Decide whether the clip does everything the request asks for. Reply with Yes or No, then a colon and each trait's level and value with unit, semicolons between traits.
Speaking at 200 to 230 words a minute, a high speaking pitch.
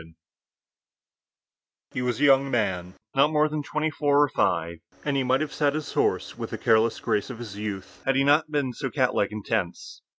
No: fast, 205 wpm; low, 130 Hz